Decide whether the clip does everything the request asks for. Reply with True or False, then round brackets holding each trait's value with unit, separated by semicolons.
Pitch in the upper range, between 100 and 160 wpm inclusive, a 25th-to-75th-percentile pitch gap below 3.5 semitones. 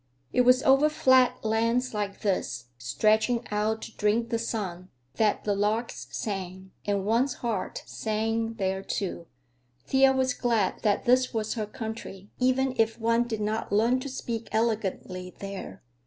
True (220 Hz; 150 wpm; 3.0 semitones)